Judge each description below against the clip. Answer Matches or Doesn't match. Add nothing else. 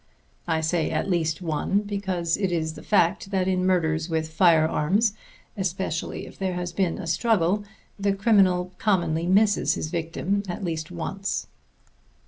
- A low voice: Doesn't match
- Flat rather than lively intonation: Doesn't match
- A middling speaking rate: Matches